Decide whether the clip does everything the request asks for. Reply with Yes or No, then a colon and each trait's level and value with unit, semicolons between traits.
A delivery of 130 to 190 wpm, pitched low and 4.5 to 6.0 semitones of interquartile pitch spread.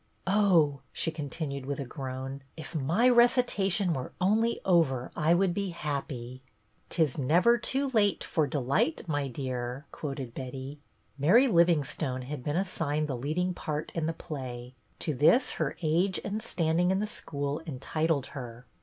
No: average, 170 wpm; medium, 155 Hz; average, 5.0 semitones